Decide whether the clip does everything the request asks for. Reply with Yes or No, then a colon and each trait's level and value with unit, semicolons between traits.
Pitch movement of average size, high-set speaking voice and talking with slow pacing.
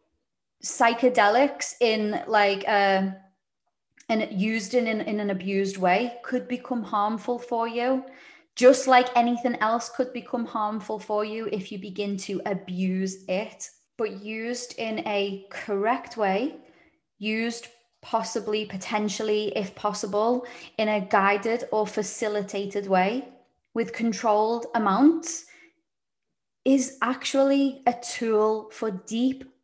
Yes: average, 3.0 semitones; high, 220 Hz; slow, 115 wpm